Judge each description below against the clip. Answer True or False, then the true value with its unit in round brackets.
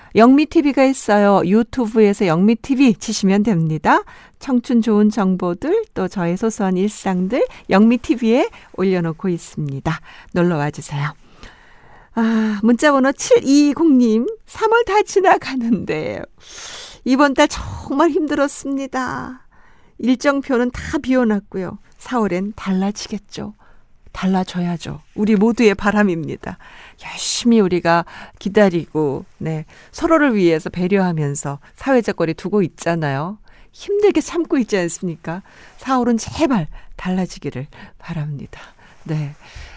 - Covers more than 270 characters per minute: False (260 characters per minute)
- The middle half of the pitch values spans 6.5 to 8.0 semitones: True (7.3 semitones)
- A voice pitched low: False (215 Hz)